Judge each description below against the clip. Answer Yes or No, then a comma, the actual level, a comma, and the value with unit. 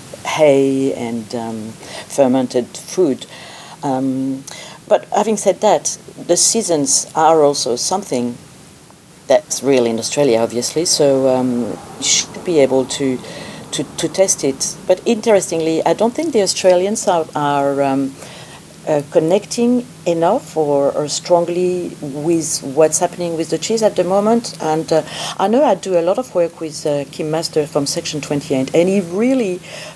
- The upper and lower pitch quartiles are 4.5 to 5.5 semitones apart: Yes, average, 4.8 semitones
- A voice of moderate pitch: Yes, medium, 160 Hz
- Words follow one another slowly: No, average, 150 wpm